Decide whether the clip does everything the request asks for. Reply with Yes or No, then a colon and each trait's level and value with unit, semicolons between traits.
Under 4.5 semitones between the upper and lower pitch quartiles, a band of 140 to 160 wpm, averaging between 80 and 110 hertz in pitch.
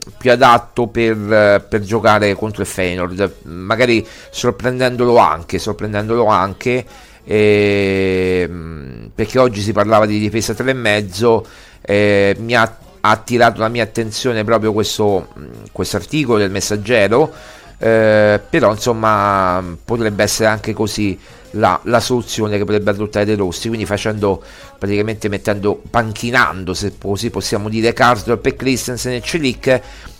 No: narrow, 2.5 semitones; average, 125 wpm; low, 105 Hz